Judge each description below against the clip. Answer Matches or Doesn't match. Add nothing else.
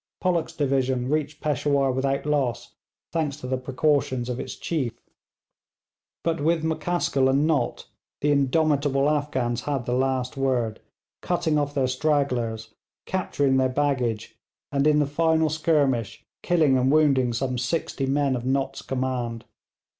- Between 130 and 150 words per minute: Matches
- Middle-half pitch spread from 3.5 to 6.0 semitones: Doesn't match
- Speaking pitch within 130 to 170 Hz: Matches